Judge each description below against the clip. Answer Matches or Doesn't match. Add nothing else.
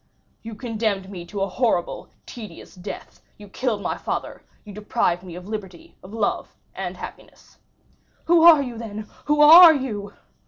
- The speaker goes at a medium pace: Matches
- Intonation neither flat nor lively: Matches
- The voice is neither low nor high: Doesn't match